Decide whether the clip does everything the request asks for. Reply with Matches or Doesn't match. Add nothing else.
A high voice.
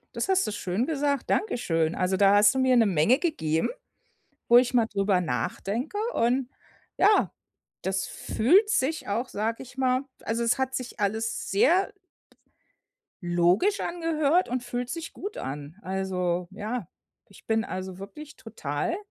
Matches